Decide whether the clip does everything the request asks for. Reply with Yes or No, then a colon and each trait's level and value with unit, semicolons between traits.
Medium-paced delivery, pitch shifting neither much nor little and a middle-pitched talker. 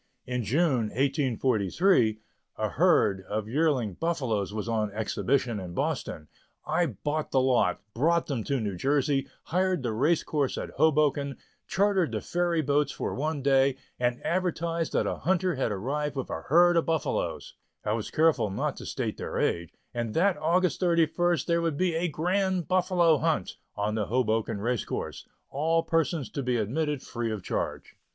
No: average, 170 wpm; wide, 6.1 semitones; medium, 145 Hz